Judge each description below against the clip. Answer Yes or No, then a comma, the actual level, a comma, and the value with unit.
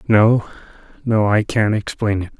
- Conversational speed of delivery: Yes, average, 150 wpm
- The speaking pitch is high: No, low, 105 Hz